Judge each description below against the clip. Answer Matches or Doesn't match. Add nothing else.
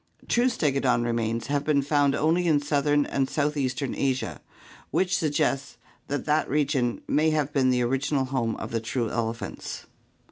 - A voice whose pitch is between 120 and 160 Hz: Matches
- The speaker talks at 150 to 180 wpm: Matches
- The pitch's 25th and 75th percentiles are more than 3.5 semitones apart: Doesn't match